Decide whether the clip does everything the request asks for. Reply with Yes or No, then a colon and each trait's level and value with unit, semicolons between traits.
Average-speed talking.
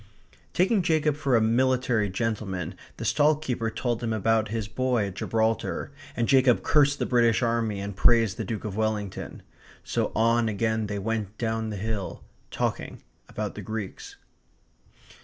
Yes: average, 160 wpm